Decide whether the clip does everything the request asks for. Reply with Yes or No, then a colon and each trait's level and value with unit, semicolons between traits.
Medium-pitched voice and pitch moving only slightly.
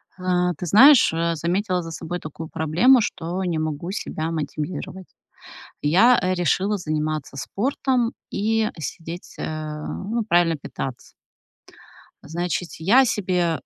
No: medium, 175 Hz; average, 3.8 semitones